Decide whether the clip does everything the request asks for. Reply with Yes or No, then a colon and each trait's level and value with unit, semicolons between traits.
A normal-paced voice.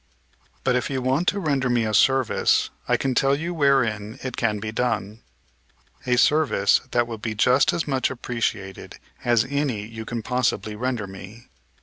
Yes: average, 170 wpm